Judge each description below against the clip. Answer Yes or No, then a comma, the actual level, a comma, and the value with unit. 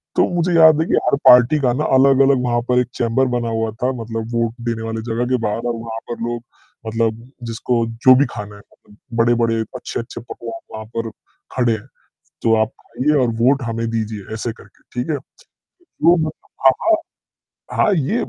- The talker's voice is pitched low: Yes, low, 120 Hz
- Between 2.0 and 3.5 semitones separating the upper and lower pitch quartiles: Yes, narrow, 2.6 semitones